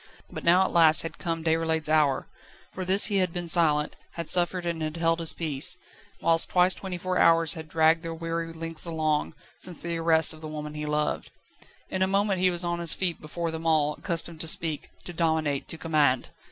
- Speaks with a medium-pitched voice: Yes, medium, 165 Hz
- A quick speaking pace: Yes, fast, 210 wpm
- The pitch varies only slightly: Yes, narrow, 1.6 semitones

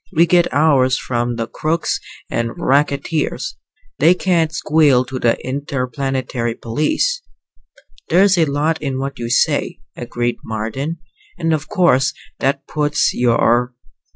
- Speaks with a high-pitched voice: No, medium, 140 Hz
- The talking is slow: Yes, slow, 125 wpm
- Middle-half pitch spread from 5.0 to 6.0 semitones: No, average, 4.5 semitones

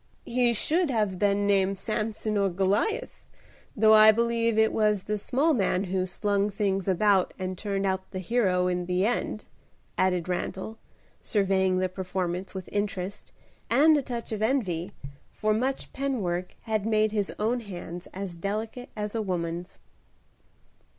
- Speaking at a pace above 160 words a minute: No, average, 155 wpm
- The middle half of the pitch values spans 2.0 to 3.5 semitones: Yes, average, 2.9 semitones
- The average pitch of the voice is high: Yes, high, 205 Hz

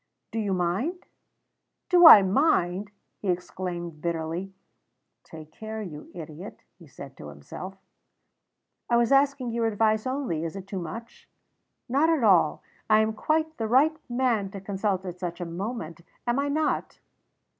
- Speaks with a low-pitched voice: No, high, 200 Hz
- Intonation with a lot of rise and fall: Yes, wide, 5.7 semitones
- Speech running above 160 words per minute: No, average, 155 wpm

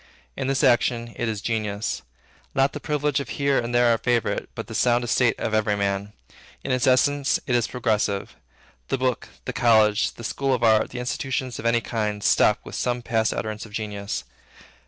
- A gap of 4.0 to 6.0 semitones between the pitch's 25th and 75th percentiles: No, average, 2.9 semitones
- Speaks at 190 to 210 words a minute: Yes, average, 195 wpm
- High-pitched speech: No, low, 120 Hz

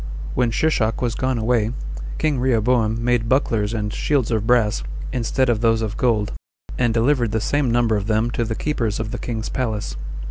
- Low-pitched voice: Yes, low, 115 Hz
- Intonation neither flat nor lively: No, narrow, 2.1 semitones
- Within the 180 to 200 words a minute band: Yes, average, 190 wpm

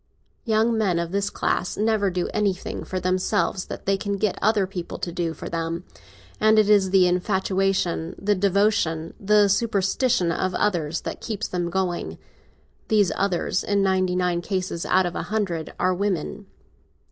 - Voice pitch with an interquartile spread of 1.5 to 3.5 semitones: Yes, narrow, 2.5 semitones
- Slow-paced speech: No, average, 165 wpm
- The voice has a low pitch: No, high, 190 Hz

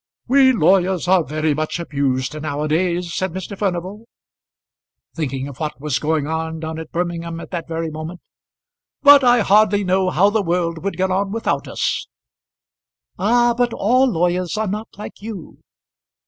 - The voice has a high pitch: No, medium, 180 Hz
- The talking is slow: No, average, 165 wpm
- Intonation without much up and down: No, average, 4.3 semitones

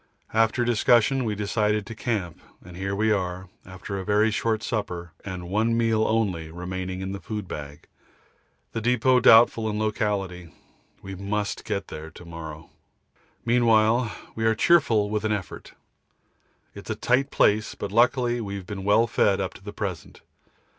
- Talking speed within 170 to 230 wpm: No, average, 160 wpm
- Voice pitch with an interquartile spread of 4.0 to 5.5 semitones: No, average, 3.2 semitones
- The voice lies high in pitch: No, low, 105 Hz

